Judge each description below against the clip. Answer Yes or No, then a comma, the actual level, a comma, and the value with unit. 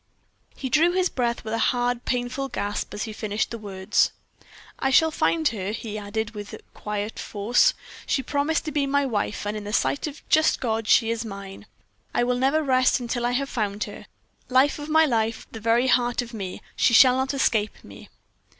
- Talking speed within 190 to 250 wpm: Yes, fast, 205 wpm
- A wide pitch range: No, average, 4.1 semitones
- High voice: Yes, high, 240 Hz